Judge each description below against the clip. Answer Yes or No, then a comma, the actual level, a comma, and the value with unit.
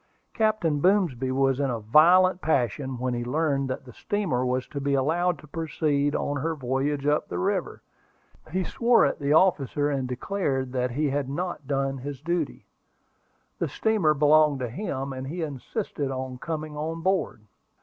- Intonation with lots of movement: No, average, 3.8 semitones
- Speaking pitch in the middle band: Yes, medium, 145 Hz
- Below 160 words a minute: No, average, 170 wpm